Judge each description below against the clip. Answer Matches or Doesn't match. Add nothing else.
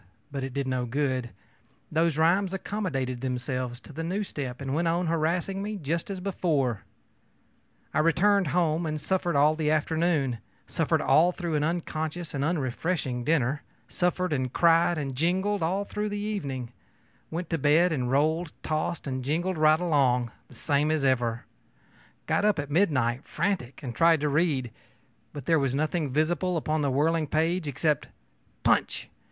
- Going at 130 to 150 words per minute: Doesn't match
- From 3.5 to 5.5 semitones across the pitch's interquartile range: Matches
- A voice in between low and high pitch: Matches